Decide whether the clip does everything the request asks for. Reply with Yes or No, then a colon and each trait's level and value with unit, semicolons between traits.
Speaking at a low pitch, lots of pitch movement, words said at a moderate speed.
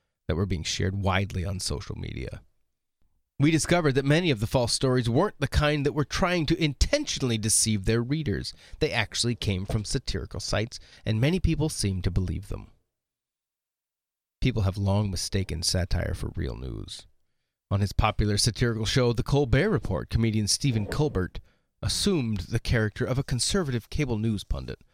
Yes: low, 115 Hz; wide, 5.9 semitones; average, 165 wpm